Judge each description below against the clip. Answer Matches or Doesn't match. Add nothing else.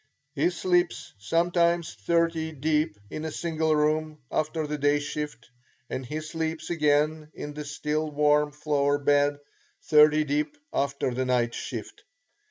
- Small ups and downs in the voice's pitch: Matches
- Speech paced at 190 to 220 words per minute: Doesn't match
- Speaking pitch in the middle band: Matches